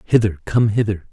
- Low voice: Yes, low, 100 Hz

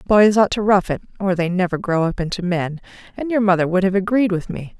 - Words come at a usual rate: No, fast, 250 wpm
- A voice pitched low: No, high, 190 Hz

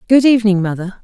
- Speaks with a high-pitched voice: Yes, high, 210 Hz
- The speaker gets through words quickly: No, average, 175 wpm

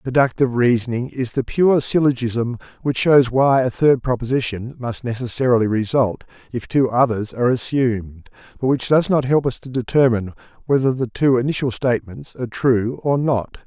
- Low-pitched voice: Yes, low, 125 Hz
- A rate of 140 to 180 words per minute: Yes, average, 160 wpm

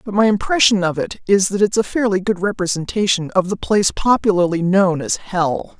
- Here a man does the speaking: No, female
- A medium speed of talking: Yes, average, 195 wpm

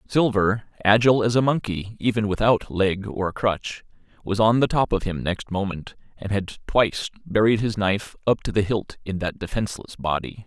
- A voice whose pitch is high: No, low, 105 Hz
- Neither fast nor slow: Yes, average, 185 wpm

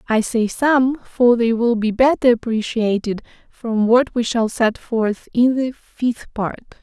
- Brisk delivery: No, average, 165 wpm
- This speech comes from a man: No, female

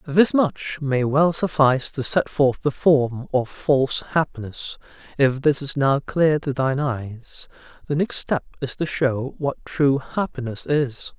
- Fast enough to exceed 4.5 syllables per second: No, 4.0 syllables/s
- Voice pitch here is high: No, medium, 140 Hz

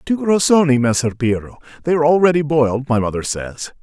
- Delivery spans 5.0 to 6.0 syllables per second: Yes, 5.8 syllables/s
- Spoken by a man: Yes, male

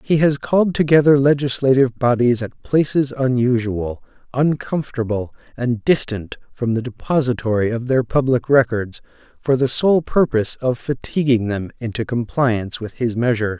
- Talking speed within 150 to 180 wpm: No, slow, 135 wpm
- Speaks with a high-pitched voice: No, low, 125 Hz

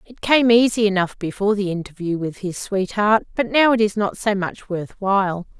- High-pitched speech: Yes, high, 205 Hz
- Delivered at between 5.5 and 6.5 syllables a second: No, 5.1 syllables/s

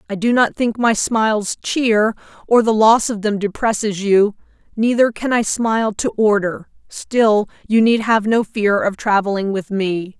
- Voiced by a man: No, female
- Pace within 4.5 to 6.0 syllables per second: No, 4.3 syllables/s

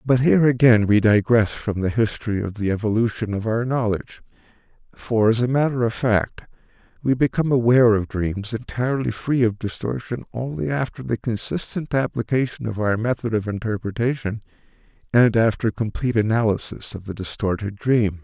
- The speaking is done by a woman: No, male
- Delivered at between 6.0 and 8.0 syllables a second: No, 5.4 syllables/s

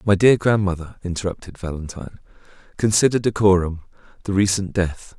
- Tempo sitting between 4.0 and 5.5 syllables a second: No, 5.7 syllables/s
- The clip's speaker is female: No, male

